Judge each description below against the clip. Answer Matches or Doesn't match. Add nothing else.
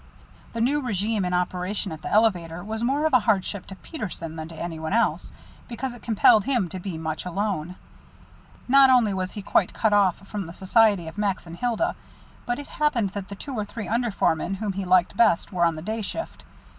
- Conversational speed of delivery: Doesn't match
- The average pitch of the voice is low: Doesn't match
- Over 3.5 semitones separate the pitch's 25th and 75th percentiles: Matches